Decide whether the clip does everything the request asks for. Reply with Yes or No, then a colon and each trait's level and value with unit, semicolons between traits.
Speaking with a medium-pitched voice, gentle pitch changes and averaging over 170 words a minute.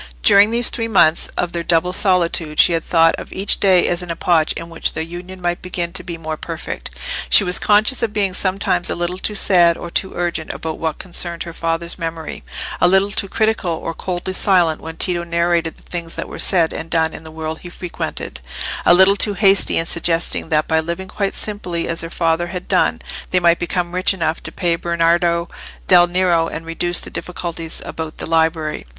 Yes: medium, 170 Hz; narrow, 1.9 semitones; fast, 205 wpm